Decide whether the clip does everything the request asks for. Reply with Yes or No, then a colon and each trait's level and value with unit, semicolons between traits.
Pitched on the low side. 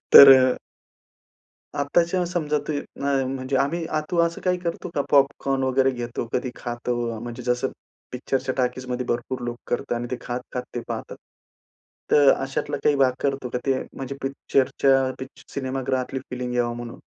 Yes: low, 130 Hz